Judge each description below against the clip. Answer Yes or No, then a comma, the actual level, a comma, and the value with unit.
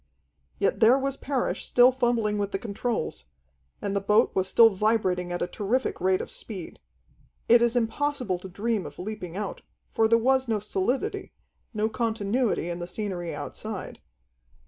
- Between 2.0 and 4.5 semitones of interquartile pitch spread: Yes, average, 3.9 semitones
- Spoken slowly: No, average, 165 wpm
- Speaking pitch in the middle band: No, high, 215 Hz